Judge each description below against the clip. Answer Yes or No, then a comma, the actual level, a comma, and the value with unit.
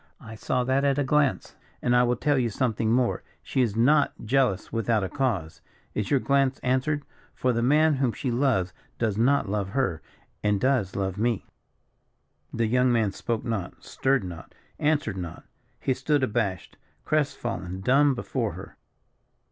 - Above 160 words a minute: Yes, average, 170 wpm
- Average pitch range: Yes, average, 4.4 semitones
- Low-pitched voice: Yes, low, 120 Hz